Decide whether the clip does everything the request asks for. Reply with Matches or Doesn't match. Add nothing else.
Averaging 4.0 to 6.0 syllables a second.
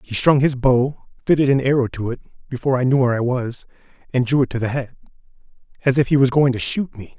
Doesn't match